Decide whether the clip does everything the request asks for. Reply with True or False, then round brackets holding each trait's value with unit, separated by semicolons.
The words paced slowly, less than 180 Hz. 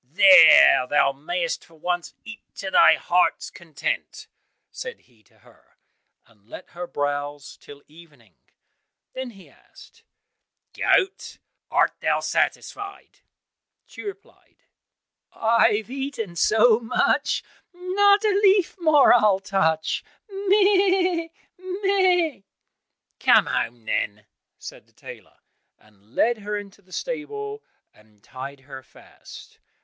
False (115 wpm; 210 Hz)